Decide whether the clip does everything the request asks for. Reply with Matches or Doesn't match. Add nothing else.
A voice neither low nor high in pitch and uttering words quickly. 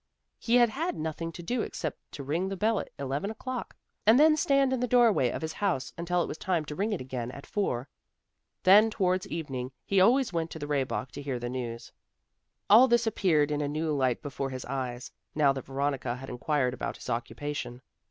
Matches